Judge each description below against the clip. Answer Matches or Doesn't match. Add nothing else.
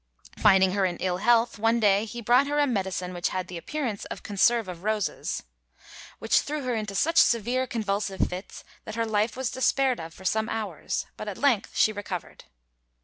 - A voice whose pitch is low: Doesn't match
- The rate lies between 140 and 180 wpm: Doesn't match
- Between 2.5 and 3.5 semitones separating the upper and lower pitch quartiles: Doesn't match